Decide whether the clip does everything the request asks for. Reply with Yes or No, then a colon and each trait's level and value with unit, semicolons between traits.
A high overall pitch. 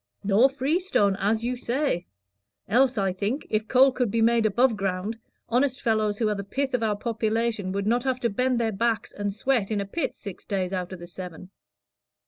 Yes: high, 220 Hz